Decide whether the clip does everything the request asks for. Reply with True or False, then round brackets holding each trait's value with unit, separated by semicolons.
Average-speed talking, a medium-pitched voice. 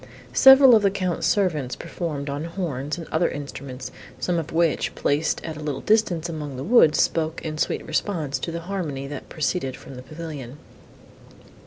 True (175 wpm; 160 Hz)